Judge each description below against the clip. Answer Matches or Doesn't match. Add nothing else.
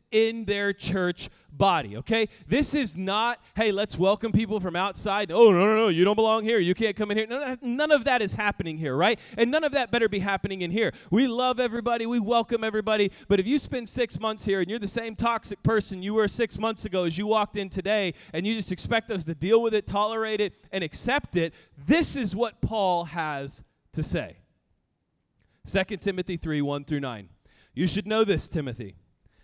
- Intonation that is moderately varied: Matches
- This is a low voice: Doesn't match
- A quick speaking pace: Matches